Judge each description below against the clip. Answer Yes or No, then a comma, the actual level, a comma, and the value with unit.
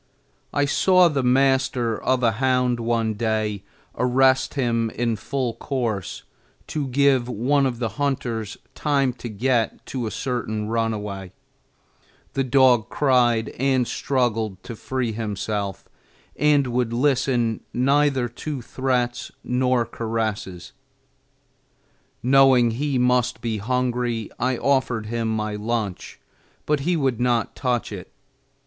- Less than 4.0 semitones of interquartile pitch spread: Yes, average, 2.8 semitones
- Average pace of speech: No, slow, 125 wpm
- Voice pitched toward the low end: Yes, low, 125 Hz